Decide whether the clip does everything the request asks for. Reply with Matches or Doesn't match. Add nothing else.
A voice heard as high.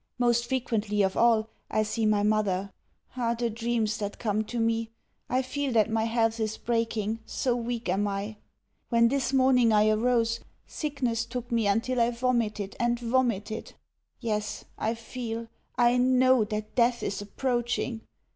Matches